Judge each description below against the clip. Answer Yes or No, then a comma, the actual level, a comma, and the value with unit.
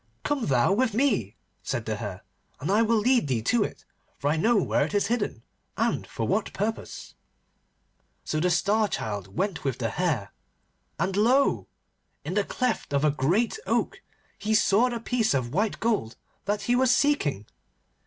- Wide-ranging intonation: Yes, wide, 8.1 semitones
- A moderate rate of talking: Yes, average, 180 wpm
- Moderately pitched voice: No, high, 205 Hz